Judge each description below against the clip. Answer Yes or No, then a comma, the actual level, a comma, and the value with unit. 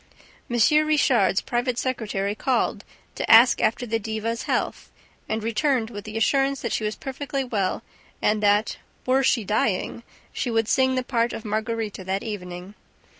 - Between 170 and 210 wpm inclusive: No, average, 160 wpm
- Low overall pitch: No, high, 225 Hz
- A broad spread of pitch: No, average, 3.1 semitones